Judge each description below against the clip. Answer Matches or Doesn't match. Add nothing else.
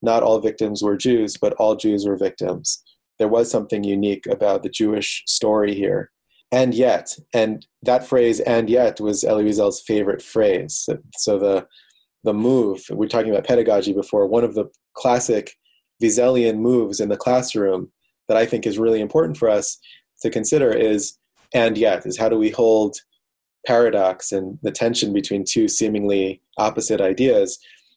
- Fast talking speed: Doesn't match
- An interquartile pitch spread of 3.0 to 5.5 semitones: Doesn't match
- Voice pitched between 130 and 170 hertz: Doesn't match